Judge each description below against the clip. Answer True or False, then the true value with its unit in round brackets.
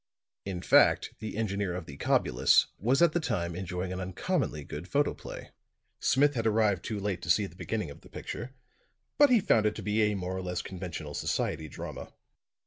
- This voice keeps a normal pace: True (195 wpm)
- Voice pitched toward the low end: True (100 Hz)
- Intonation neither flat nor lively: True (4.0 semitones)